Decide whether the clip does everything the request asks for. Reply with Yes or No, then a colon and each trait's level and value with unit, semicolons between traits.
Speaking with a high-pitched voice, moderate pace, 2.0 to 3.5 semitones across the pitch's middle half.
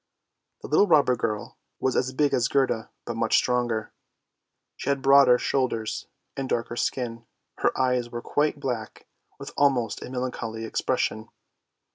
No: low, 125 Hz; average, 145 wpm; average, 2.7 semitones